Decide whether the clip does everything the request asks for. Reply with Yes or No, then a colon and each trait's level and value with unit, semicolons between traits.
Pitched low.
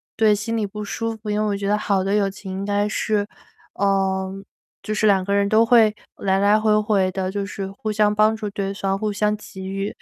No: high, 205 Hz